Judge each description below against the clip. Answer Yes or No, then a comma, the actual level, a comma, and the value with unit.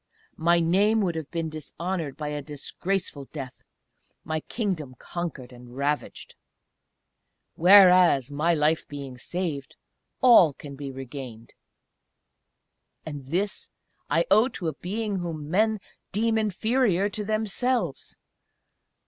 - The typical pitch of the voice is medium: Yes, medium, 165 Hz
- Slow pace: Yes, slow, 115 wpm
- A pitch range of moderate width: No, wide, 5.7 semitones